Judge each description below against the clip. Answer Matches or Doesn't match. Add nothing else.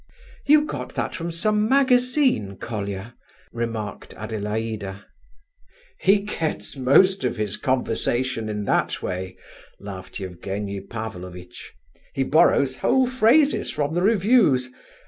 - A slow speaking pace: Matches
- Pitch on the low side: Matches